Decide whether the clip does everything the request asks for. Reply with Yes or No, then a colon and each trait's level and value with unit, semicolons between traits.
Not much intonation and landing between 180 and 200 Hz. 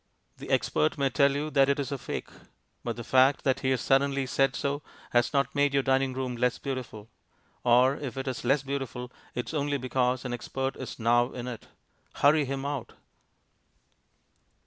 No: narrow, 2.0 semitones; low, 135 Hz